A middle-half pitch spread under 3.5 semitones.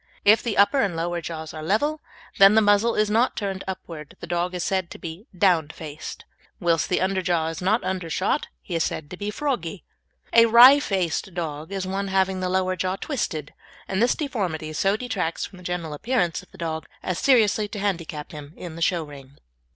No: average, 3.9 semitones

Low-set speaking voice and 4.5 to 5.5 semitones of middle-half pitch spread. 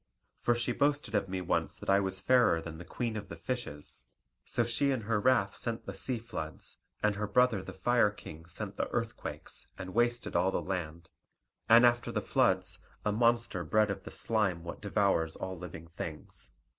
Yes: low, 105 Hz; average, 5.2 semitones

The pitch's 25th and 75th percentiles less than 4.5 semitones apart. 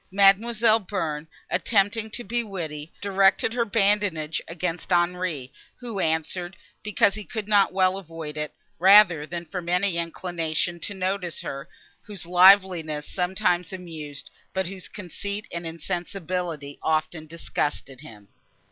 Yes: average, 3.5 semitones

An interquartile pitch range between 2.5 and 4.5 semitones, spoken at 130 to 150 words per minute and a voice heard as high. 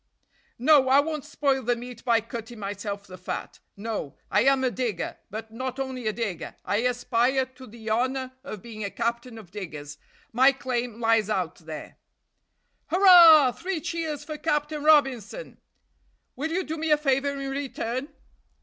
No: average, 4.2 semitones; average, 165 wpm; very high, 250 Hz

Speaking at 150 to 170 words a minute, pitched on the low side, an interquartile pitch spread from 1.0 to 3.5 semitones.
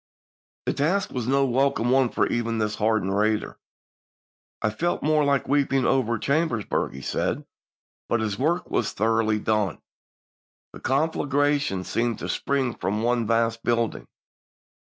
No: average, 155 wpm; low, 120 Hz; average, 4.1 semitones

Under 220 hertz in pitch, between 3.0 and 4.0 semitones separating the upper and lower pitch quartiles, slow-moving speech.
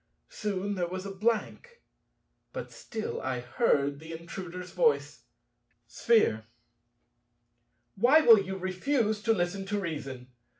No: high, 190 Hz; average, 4.8 semitones; slow, 120 wpm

